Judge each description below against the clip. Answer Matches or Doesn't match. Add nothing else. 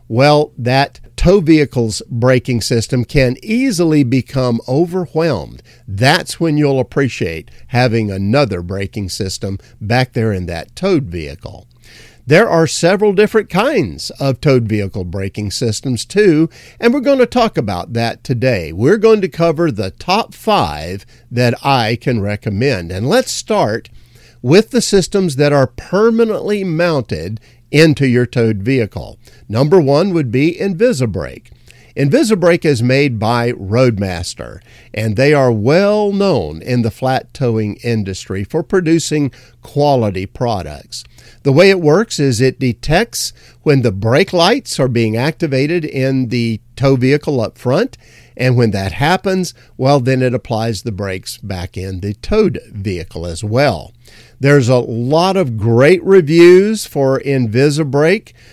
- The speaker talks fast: Doesn't match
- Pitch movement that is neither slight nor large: Doesn't match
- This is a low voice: Matches